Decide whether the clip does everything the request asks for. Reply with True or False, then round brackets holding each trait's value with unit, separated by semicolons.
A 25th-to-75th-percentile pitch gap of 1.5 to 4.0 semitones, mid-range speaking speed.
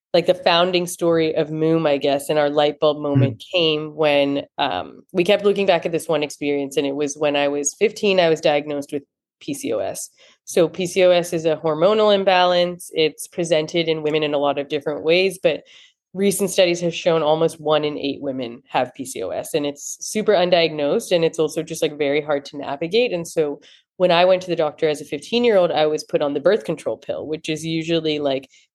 False (3.1 semitones; 215 wpm)